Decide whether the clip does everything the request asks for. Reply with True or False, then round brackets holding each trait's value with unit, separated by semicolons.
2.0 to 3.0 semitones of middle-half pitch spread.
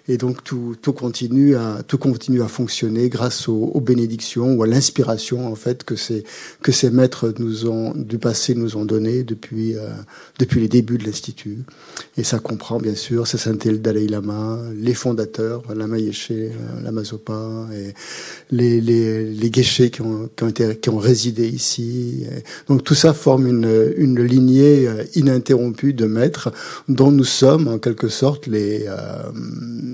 True (2.4 semitones)